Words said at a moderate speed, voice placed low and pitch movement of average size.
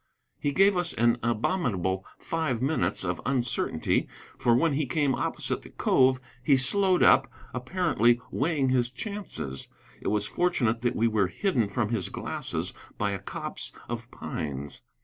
No: average, 150 wpm; low, 125 Hz; wide, 6.0 semitones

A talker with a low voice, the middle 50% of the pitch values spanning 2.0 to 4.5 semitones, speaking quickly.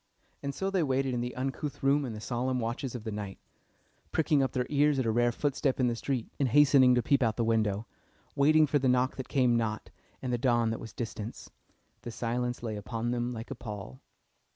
Yes: low, 125 Hz; average, 3.0 semitones; fast, 225 wpm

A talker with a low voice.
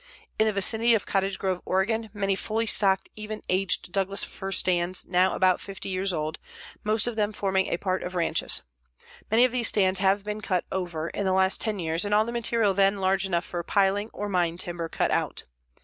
No: high, 195 Hz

